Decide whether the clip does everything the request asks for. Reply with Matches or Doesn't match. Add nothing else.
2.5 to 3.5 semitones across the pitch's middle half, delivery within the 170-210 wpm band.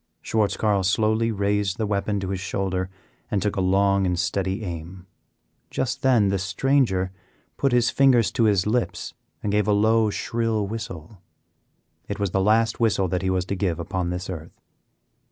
Matches